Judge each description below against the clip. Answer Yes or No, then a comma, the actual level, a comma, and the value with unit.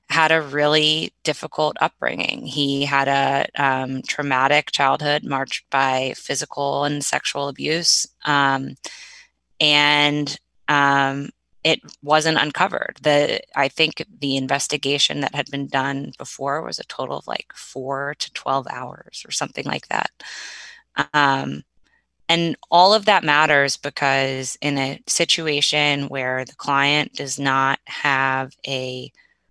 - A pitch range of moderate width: No, narrow, 1.7 semitones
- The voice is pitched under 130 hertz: No, medium, 140 Hz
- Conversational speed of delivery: No, slow, 130 wpm